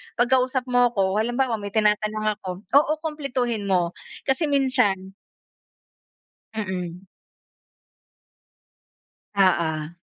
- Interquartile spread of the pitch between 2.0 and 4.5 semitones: No, average, 5.2 semitones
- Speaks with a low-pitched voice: No, high, 215 Hz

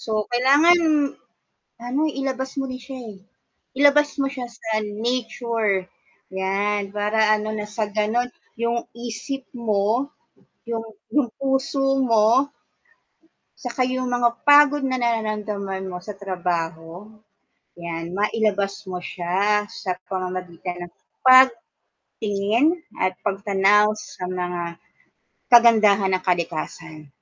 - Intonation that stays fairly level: No, average, 4.2 semitones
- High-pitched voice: Yes, high, 215 Hz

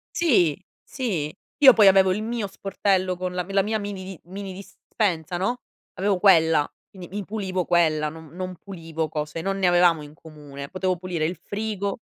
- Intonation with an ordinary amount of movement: Yes, average, 3.4 semitones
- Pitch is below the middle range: No, medium, 185 Hz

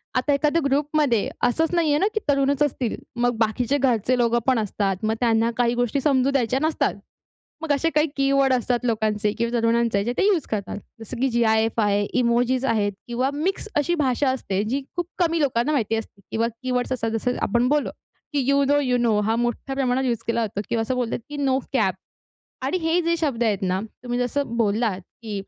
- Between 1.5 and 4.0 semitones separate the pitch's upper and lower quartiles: Yes, average, 3.6 semitones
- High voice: Yes, high, 245 Hz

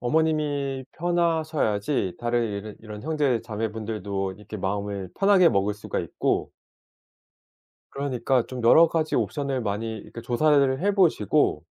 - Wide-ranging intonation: Yes, wide, 6.6 semitones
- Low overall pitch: Yes, low, 120 Hz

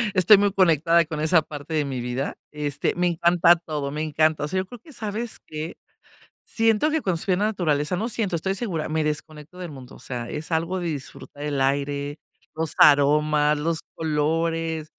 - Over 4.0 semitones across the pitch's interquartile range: No, average, 3.2 semitones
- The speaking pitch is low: No, medium, 160 Hz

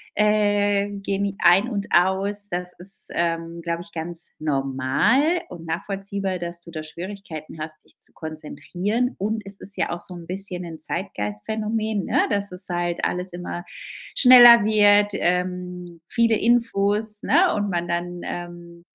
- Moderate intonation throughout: Yes, average, 3.1 semitones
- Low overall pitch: No, medium, 185 Hz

